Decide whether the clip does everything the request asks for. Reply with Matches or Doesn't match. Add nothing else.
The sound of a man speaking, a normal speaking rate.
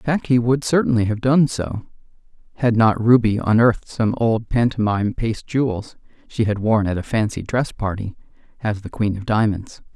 Matches